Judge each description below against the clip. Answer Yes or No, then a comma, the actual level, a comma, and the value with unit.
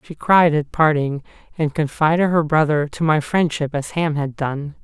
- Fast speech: No, average, 185 wpm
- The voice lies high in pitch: No, medium, 155 Hz